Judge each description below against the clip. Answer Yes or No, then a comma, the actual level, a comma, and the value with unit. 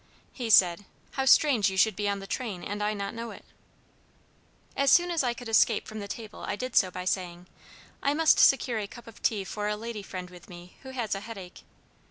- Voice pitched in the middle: No, high, 210 Hz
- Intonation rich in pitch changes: No, average, 3.7 semitones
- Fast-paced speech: Yes, fast, 235 wpm